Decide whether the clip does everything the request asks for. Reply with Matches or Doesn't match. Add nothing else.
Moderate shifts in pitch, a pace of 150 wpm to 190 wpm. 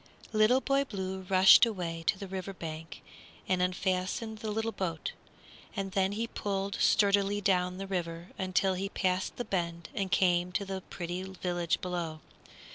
Doesn't match